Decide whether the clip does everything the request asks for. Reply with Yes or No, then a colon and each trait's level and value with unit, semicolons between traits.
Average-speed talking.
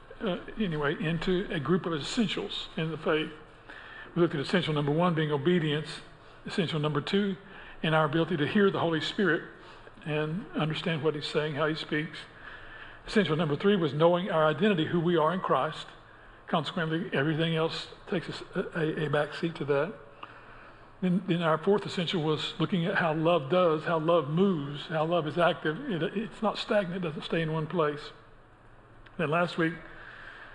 Yes: average, 180 wpm